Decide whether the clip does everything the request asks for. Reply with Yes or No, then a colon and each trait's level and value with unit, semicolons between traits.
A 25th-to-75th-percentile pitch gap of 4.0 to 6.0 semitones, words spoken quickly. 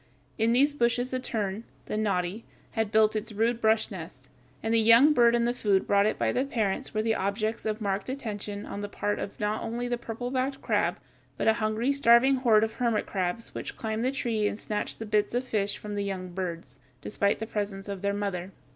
No: average, 2.7 semitones; fast, 220 wpm